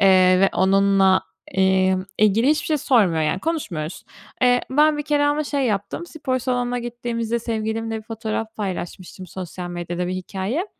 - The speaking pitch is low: No, high, 220 Hz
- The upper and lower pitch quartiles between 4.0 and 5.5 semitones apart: Yes, average, 4.8 semitones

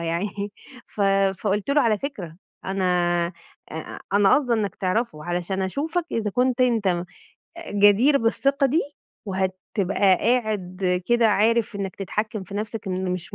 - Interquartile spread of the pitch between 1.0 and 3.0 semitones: No, average, 3.8 semitones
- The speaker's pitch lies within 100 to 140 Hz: No, high, 205 Hz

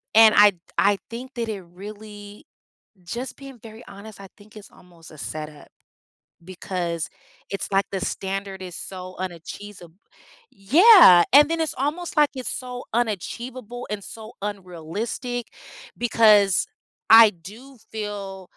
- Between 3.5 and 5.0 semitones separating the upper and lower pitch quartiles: Yes, average, 4.2 semitones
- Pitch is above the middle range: Yes, high, 205 Hz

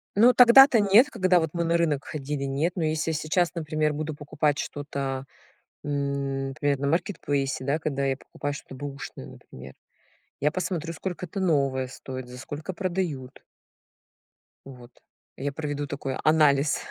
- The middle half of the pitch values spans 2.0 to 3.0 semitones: No, average, 3.4 semitones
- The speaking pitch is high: No, medium, 145 Hz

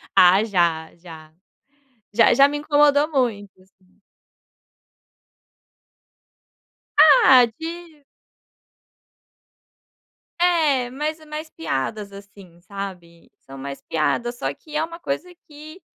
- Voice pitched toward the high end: Yes, high, 245 Hz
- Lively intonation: Yes, wide, 8.7 semitones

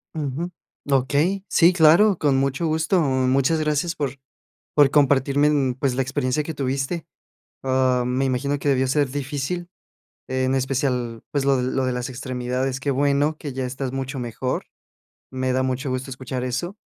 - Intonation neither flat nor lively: No, narrow, 2.2 semitones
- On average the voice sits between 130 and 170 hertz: Yes, low, 135 Hz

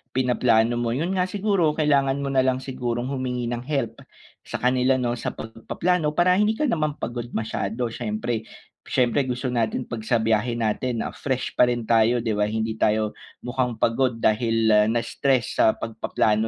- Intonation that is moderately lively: Yes, average, 3.0 semitones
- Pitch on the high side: No, low, 120 Hz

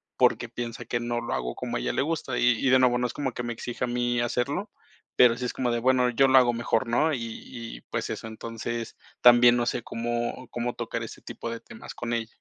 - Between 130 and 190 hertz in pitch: No, low, 120 Hz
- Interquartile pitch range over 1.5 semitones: No, narrow, 1.1 semitones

